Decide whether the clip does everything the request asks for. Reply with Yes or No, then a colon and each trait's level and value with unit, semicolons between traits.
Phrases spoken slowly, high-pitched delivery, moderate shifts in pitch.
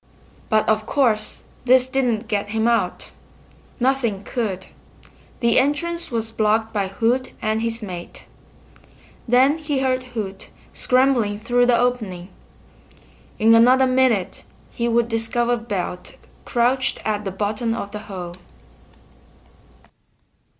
Yes: slow, 120 wpm; high, 230 Hz; average, 3.1 semitones